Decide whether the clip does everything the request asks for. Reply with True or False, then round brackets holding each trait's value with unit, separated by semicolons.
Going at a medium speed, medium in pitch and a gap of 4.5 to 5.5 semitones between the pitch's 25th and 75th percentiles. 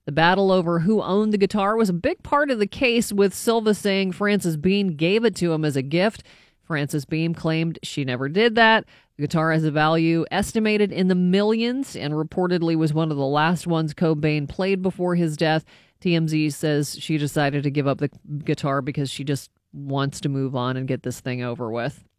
False (210 wpm; 165 Hz; 4.9 semitones)